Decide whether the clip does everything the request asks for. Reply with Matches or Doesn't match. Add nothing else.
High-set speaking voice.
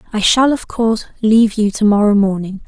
Matches